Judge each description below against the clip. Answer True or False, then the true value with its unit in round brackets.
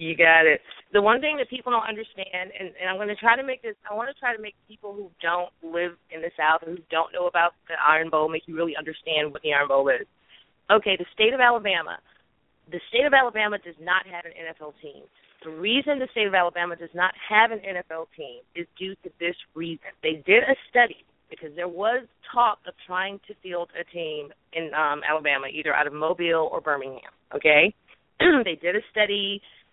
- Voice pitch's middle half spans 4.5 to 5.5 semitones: True (4.8 semitones)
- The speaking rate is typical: False (220 wpm)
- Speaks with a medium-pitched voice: True (180 Hz)